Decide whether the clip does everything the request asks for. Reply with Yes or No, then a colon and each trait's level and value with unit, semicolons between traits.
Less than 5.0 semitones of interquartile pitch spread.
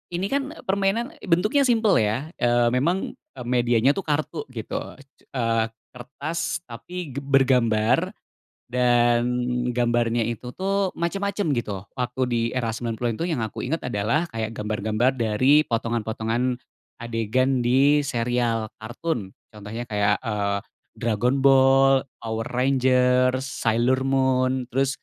Yes: average, 3.5 semitones